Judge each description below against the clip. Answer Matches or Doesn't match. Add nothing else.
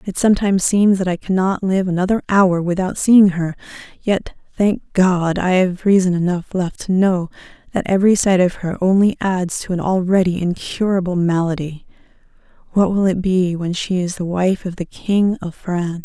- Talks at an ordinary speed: Matches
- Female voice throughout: Matches